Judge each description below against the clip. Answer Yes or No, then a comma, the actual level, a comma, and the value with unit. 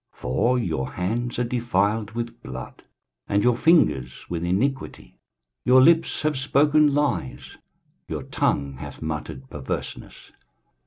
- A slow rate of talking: Yes, slow, 125 wpm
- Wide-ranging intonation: Yes, wide, 8.9 semitones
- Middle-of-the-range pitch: No, low, 115 Hz